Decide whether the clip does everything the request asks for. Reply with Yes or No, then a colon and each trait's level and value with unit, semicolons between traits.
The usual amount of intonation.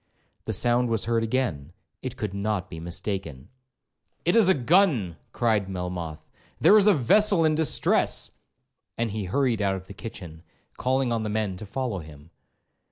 No: wide, 6.0 semitones